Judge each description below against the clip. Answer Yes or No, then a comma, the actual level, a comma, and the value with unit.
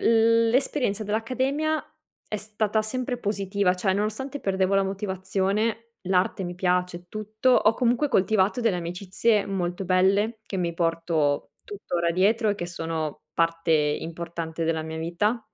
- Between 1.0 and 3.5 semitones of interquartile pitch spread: No, average, 4.2 semitones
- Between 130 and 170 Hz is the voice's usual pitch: No, high, 195 Hz